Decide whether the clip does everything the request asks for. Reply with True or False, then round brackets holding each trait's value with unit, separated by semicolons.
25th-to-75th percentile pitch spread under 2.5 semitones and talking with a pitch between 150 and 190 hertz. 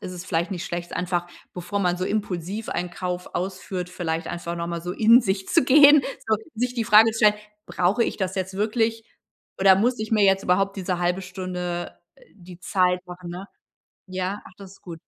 False (2.9 semitones; 185 Hz)